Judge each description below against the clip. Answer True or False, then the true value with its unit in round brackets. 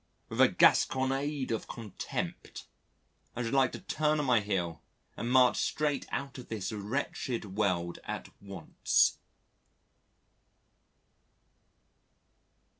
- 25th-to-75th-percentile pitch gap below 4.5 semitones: False (5.0 semitones)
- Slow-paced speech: True (110 wpm)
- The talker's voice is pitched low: True (120 Hz)